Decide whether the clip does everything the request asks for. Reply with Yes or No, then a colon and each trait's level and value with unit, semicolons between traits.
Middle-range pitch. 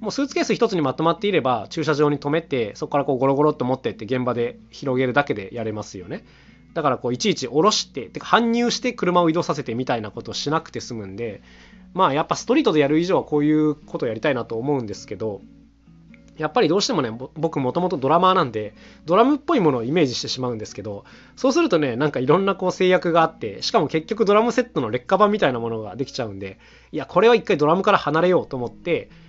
Yes: medium, 150 Hz